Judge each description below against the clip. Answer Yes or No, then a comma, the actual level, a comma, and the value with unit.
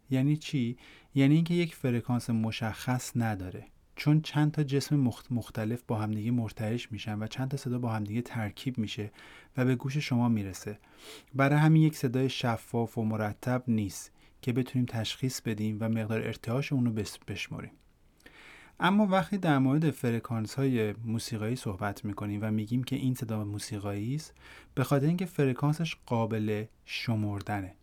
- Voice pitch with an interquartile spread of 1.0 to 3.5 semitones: No, average, 3.9 semitones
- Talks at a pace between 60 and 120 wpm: No, average, 150 wpm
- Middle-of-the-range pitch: No, low, 120 Hz